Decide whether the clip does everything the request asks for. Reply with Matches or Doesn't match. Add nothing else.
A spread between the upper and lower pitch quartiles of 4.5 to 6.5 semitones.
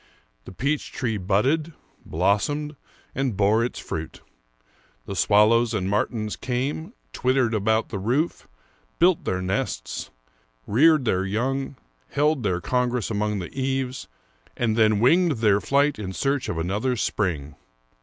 Matches